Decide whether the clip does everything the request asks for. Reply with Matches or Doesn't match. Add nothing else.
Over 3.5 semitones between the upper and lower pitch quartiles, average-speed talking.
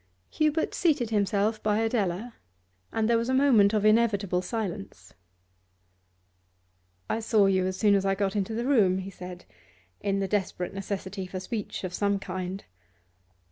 Doesn't match